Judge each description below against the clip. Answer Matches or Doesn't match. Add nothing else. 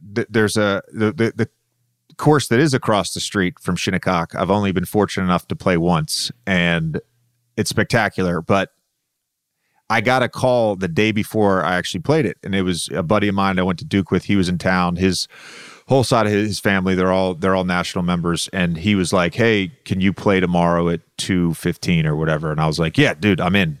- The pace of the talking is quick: Matches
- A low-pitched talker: Matches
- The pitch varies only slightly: Doesn't match